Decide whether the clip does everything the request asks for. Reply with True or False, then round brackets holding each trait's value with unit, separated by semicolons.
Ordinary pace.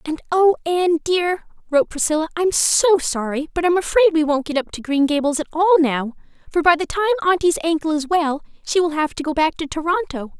False (220 wpm)